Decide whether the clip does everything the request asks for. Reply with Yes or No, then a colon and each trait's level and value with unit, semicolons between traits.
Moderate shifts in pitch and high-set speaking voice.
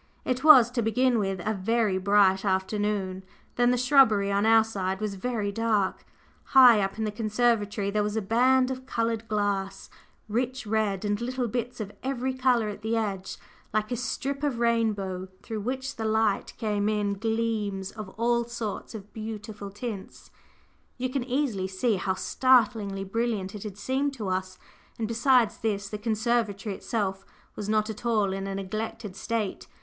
Yes: average, 3.0 semitones; high, 215 Hz